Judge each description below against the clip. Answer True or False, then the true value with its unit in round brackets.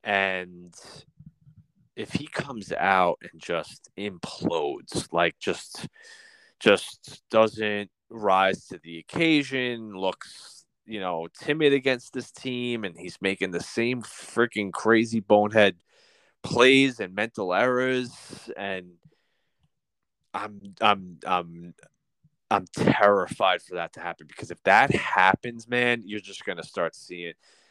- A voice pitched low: True (115 Hz)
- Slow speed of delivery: True (120 wpm)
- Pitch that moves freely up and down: True (5.7 semitones)